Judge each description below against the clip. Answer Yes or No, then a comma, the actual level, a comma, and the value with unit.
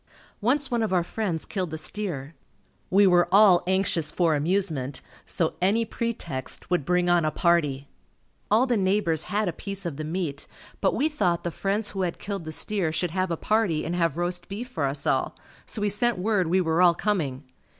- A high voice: No, medium, 180 Hz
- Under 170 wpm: No, average, 200 wpm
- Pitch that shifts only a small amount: No, average, 4.1 semitones